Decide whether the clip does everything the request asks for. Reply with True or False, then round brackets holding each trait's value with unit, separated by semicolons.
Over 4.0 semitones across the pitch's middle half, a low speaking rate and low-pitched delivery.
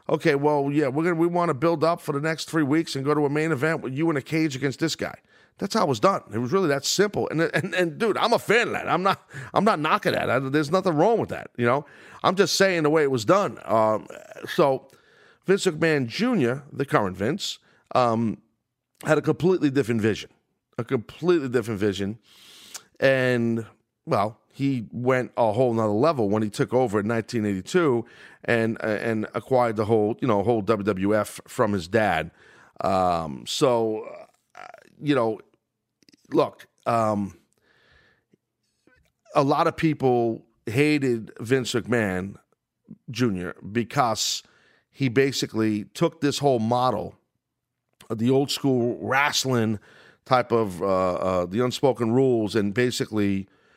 False (5.0 semitones; 165 wpm; 125 Hz)